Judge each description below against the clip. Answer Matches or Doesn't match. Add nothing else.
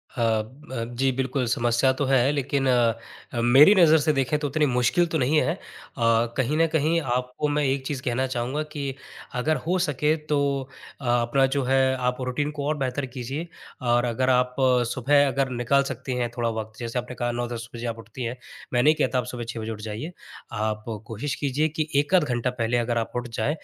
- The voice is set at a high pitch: Doesn't match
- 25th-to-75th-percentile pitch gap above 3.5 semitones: Doesn't match